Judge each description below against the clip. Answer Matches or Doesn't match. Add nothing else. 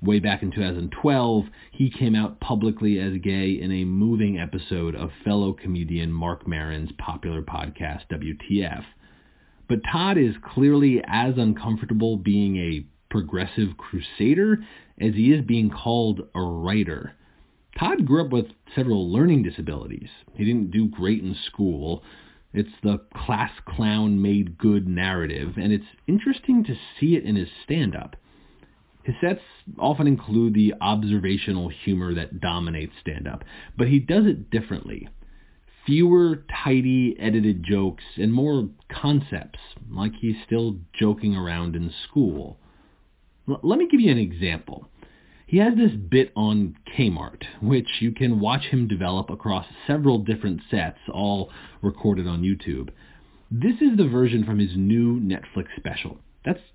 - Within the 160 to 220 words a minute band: Doesn't match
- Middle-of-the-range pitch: Doesn't match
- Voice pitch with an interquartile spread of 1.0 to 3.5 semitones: Doesn't match